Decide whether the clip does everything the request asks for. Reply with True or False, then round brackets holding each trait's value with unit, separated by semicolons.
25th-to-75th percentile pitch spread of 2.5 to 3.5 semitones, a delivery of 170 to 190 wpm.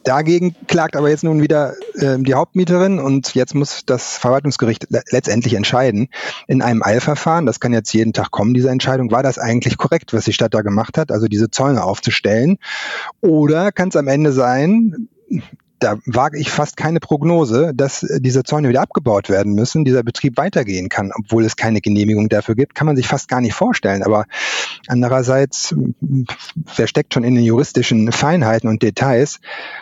False (5.1 semitones; 175 wpm)